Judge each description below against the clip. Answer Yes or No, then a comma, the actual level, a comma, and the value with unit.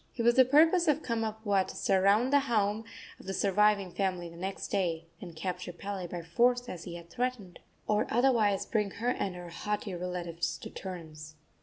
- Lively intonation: No, average, 4.6 semitones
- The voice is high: Yes, high, 200 Hz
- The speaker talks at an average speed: Yes, average, 185 wpm